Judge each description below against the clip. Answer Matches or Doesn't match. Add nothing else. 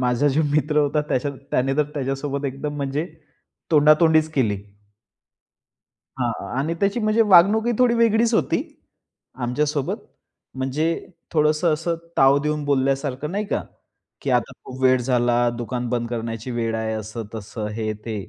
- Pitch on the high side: Doesn't match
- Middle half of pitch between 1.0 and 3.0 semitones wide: Doesn't match